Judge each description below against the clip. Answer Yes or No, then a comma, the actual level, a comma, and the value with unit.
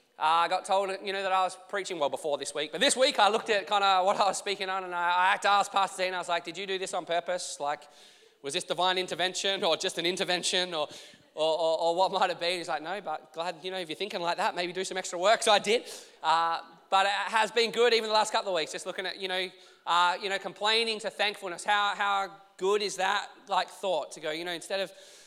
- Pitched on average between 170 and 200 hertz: Yes, medium, 185 Hz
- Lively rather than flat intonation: No, narrow, 2.5 semitones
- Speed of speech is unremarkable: No, fast, 280 wpm